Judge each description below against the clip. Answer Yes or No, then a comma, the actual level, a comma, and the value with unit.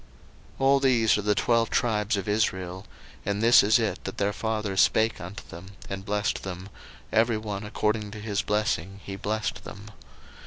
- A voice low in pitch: Yes, low, 105 Hz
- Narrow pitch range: Yes, narrow, 2.1 semitones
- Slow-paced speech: No, average, 180 wpm